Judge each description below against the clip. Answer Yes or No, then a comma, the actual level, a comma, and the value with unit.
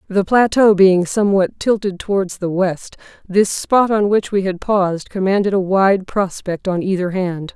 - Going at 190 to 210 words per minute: No, average, 175 wpm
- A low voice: No, high, 190 Hz